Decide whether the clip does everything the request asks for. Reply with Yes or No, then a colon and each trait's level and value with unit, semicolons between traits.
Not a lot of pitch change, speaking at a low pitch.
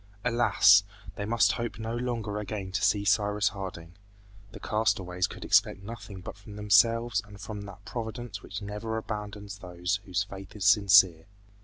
Yes: narrow, 2.1 semitones; low, 105 Hz